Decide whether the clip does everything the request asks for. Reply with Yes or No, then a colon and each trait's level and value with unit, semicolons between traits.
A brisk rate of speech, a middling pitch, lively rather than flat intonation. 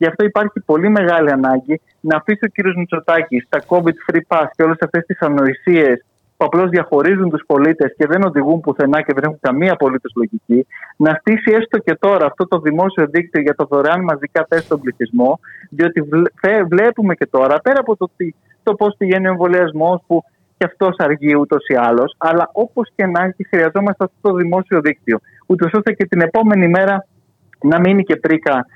No: fast, 185 wpm; medium, 170 Hz; average, 4.1 semitones